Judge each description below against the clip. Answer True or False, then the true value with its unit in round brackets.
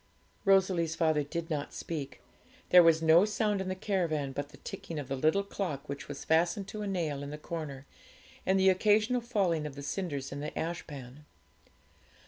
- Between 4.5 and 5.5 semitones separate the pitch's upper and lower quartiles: True (4.8 semitones)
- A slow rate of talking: False (185 wpm)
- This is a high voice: False (165 Hz)